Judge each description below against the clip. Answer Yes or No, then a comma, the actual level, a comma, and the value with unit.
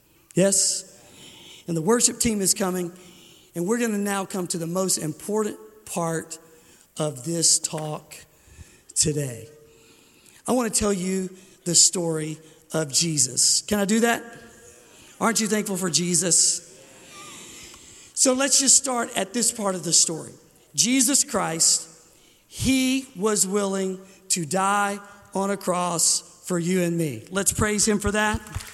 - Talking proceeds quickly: No, average, 145 wpm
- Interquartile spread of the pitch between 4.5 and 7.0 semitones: No, average, 4.0 semitones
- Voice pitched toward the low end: No, medium, 185 Hz